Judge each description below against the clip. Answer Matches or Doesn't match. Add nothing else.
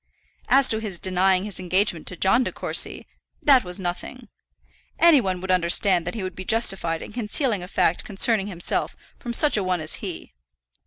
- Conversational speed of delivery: Matches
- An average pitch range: Matches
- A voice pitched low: Doesn't match